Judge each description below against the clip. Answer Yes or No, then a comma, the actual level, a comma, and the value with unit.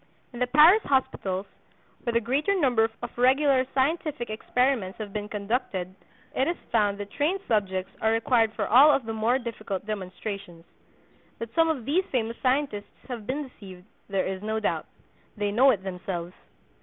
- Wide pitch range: No, average, 4.8 semitones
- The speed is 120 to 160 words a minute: No, average, 170 wpm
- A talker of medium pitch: No, high, 225 Hz